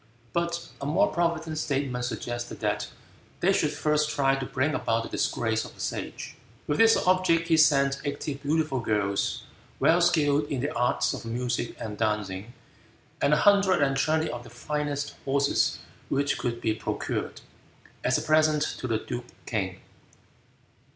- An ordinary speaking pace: Yes, average, 160 wpm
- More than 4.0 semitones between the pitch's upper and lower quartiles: Yes, average, 4.4 semitones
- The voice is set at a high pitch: No, medium, 140 Hz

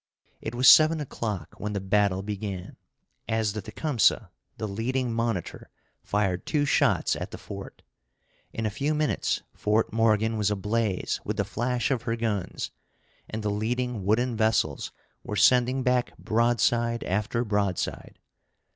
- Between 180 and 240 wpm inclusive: No, average, 145 wpm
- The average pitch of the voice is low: Yes, low, 110 Hz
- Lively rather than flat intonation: No, average, 2.8 semitones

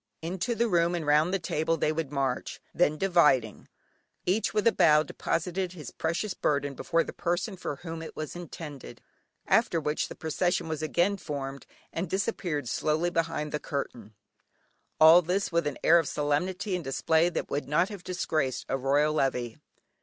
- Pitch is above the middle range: No, medium, 160 Hz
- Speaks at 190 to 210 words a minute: No, average, 175 wpm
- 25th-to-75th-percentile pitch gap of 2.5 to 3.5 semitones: Yes, average, 3.2 semitones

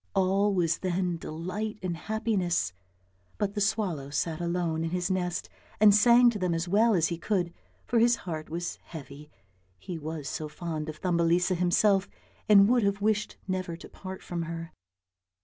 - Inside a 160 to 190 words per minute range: Yes, average, 170 wpm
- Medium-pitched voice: Yes, medium, 180 Hz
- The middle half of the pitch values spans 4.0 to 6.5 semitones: No, average, 3.5 semitones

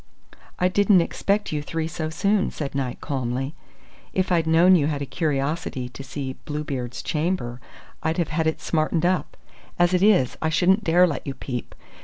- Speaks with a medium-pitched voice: Yes, medium, 160 Hz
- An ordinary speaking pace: Yes, average, 180 wpm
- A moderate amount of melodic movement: Yes, average, 4.4 semitones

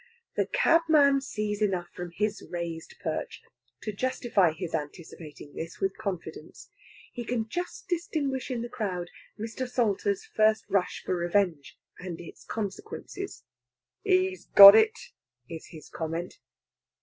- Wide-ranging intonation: Yes, wide, 7.1 semitones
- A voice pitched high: Yes, high, 210 Hz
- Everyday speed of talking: No, slow, 130 wpm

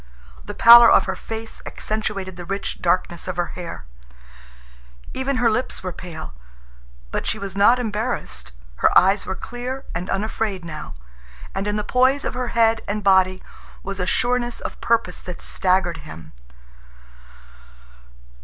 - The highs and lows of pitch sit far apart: No, average, 4.2 semitones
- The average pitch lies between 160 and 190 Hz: No, high, 200 Hz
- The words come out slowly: No, average, 150 wpm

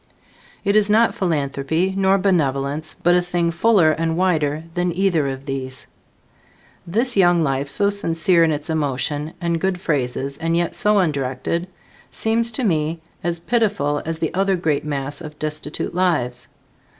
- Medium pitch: Yes, medium, 165 Hz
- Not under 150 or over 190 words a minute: Yes, average, 155 wpm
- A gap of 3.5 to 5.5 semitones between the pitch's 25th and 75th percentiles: Yes, average, 4.3 semitones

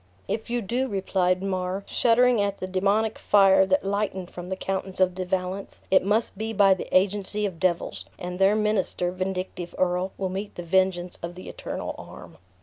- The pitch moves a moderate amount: No, narrow, 1.8 semitones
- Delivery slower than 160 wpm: No, average, 185 wpm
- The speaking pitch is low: No, high, 190 Hz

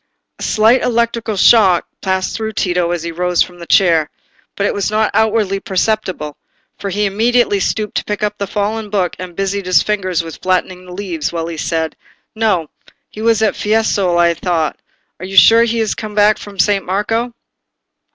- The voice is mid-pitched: No, high, 200 Hz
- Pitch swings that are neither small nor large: Yes, average, 3.3 semitones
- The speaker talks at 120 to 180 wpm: No, average, 190 wpm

